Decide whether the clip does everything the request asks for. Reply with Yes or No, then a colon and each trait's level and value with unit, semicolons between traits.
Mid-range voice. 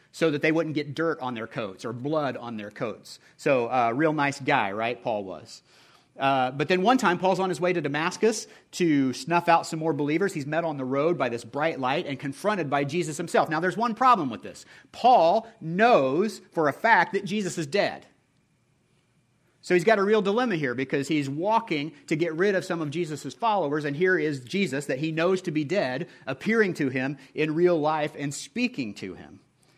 Yes: medium, 160 Hz